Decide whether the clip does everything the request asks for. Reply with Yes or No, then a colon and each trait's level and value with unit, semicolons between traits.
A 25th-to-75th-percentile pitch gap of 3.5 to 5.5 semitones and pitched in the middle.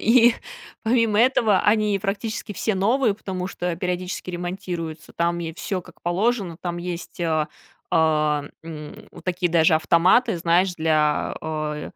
Yes: average, 3.8 semitones; medium, 180 Hz